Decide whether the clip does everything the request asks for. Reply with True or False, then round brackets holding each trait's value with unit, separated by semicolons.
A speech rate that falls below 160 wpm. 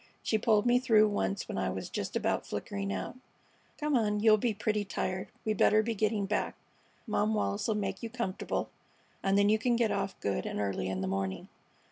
False (205 wpm)